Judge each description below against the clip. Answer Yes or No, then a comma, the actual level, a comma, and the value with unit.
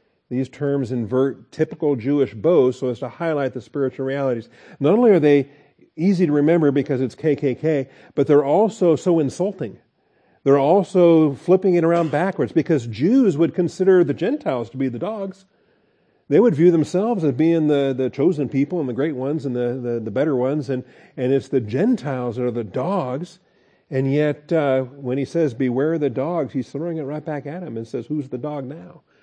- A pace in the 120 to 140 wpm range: No, average, 195 wpm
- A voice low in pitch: No, medium, 145 Hz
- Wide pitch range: No, average, 4.3 semitones